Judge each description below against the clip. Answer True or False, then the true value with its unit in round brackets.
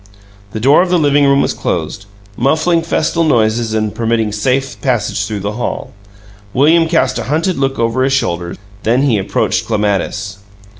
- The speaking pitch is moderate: False (125 Hz)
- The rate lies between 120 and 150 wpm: False (165 wpm)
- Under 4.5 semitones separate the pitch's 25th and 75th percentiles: False (5.0 semitones)